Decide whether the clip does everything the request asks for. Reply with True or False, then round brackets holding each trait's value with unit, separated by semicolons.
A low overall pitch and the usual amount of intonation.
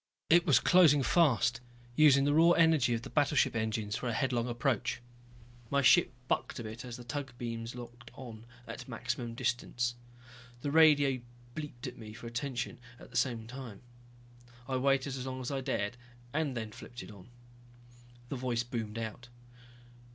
True (125 Hz; 3.0 semitones)